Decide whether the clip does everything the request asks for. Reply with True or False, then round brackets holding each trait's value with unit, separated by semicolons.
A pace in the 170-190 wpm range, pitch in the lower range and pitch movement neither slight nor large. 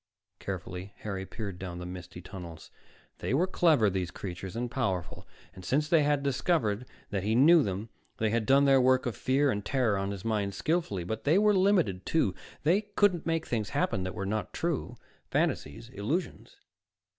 False (180 wpm; 110 Hz; 7.1 semitones)